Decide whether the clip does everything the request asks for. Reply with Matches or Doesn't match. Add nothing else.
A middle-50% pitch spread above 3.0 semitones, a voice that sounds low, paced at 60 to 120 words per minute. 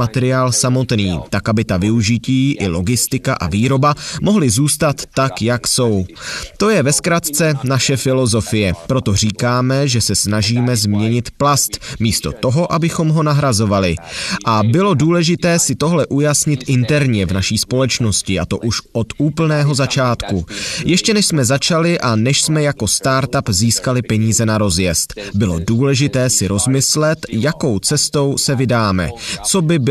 Doesn't match